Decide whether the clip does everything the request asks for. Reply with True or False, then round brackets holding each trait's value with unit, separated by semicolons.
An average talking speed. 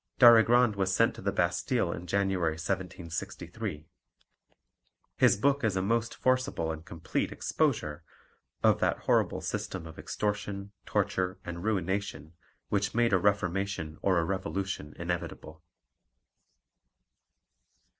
False (115 wpm)